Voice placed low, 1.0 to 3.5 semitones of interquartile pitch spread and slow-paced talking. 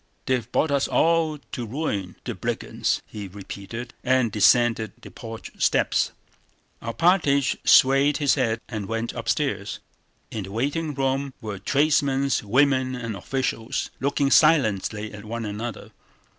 No: low, 125 Hz; average, 4.3 semitones; slow, 130 wpm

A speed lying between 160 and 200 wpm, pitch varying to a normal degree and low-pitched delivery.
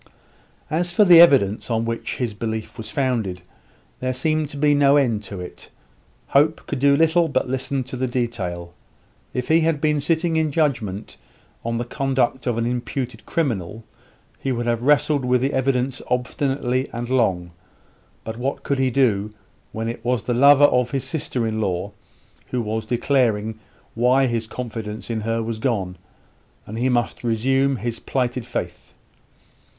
Yes: average, 165 wpm; average, 3.5 semitones; low, 125 Hz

